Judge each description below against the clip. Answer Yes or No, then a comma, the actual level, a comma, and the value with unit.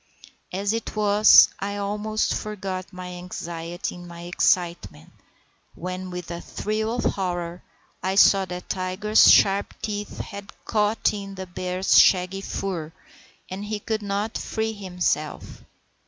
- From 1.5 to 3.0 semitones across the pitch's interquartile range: Yes, narrow, 2.5 semitones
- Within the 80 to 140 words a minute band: Yes, slow, 135 wpm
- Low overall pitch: No, high, 190 Hz